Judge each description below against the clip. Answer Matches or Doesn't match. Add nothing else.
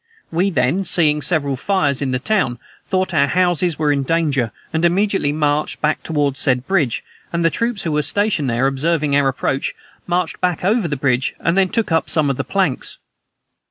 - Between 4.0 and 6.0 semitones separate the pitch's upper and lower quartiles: Matches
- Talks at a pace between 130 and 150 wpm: Doesn't match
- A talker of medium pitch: Matches